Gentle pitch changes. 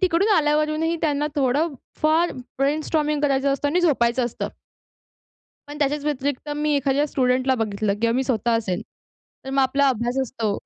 No: average, 3.0 semitones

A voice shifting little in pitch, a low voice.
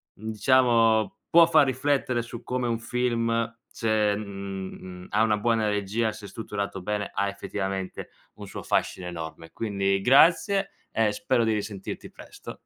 No: average, 3.0 semitones; low, 110 Hz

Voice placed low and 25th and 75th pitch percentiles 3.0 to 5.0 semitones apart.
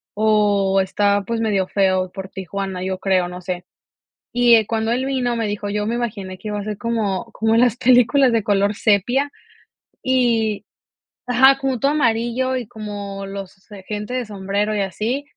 No: high, 210 Hz; average, 3.4 semitones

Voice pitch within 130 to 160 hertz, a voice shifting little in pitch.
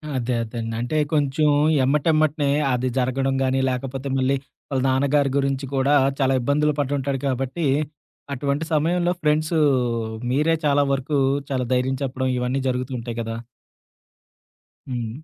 Yes: low, 135 Hz; narrow, 2.2 semitones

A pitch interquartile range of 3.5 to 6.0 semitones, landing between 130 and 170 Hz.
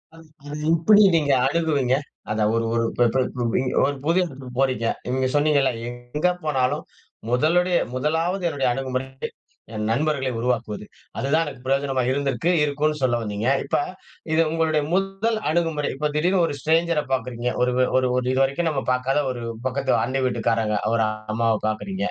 Yes: average, 4.0 semitones; low, 135 Hz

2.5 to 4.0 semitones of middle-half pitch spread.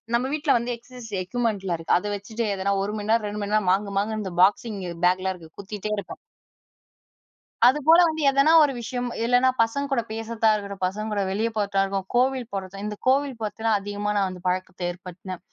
Yes: average, 3.7 semitones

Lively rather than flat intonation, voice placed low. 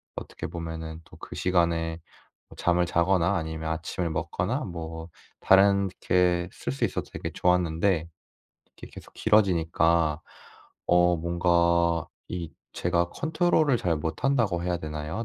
No: narrow, 1.8 semitones; very low, 85 Hz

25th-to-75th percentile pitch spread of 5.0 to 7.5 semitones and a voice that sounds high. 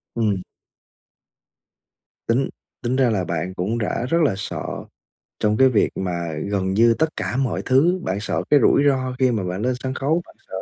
No: wide, 5.6 semitones; low, 115 Hz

